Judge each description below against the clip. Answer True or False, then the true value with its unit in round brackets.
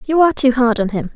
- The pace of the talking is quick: True (310 wpm)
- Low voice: False (250 Hz)